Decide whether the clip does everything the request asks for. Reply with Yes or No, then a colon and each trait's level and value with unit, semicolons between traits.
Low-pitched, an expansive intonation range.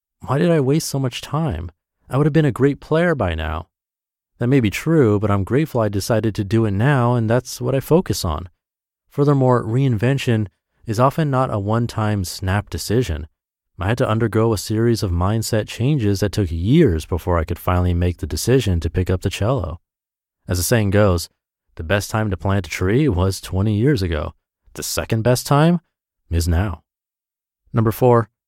Yes: low, 105 Hz; wide, 5.9 semitones